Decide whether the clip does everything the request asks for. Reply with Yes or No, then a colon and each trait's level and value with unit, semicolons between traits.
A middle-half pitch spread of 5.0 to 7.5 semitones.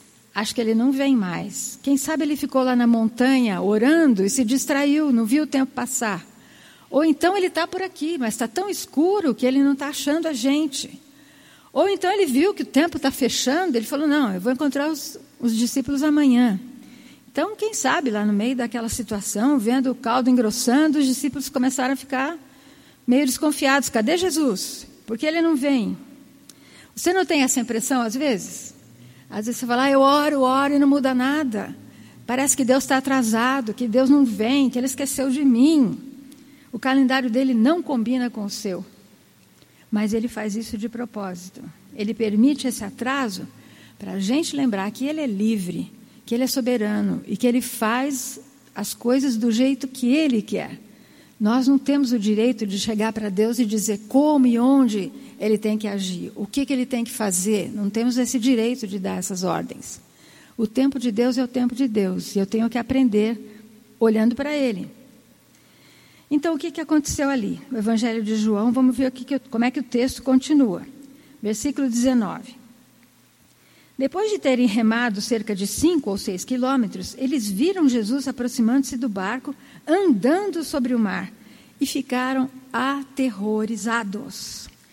No: average, 3.5 semitones